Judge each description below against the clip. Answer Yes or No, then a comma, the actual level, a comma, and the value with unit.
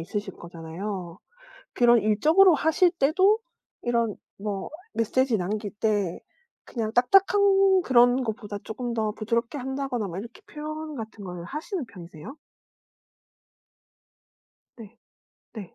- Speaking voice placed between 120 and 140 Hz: No, high, 230 Hz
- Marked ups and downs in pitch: Yes, wide, 6.3 semitones